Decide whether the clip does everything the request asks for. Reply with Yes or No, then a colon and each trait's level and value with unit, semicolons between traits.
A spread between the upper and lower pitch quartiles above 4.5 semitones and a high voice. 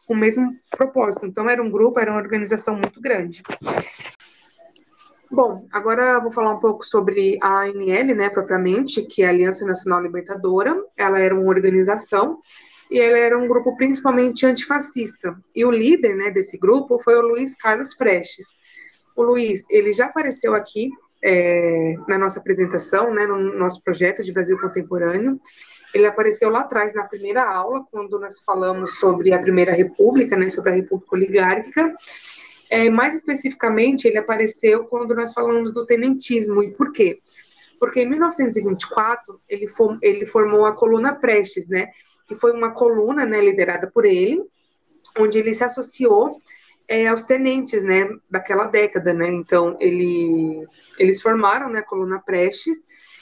Yes: average, 5.3 semitones; high, 225 Hz